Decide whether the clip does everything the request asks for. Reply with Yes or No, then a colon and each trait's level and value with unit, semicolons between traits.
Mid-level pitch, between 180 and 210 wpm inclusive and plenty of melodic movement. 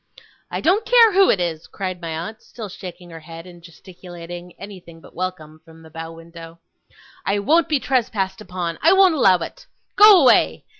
Yes: medium, 180 Hz; average, 185 wpm; wide, 7.0 semitones